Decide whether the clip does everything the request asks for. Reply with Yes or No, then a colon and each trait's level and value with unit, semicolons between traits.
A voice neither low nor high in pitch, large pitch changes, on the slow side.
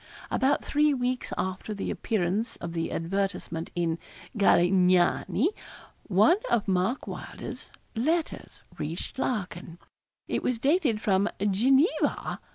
No: high, 205 Hz; wide, 6.1 semitones; slow, 110 wpm